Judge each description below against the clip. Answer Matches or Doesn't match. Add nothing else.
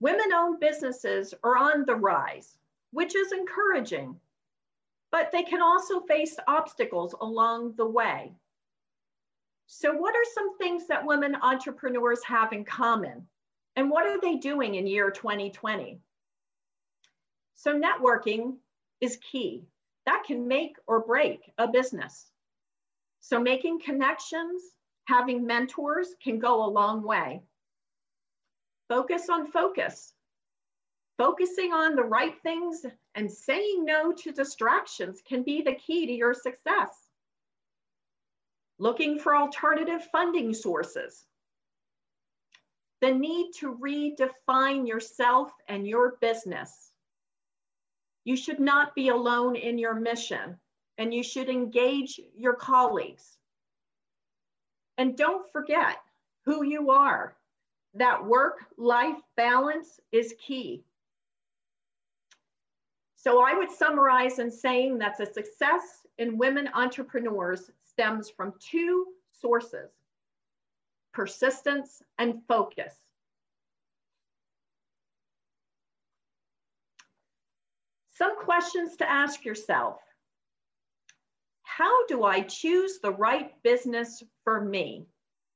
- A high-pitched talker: Matches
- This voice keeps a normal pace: Doesn't match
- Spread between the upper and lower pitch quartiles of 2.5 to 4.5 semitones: Doesn't match